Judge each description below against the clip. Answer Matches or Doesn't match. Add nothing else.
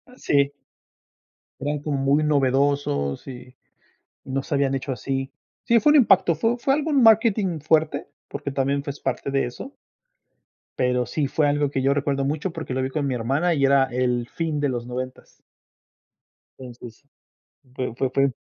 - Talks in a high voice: Doesn't match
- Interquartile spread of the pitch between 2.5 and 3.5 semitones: Matches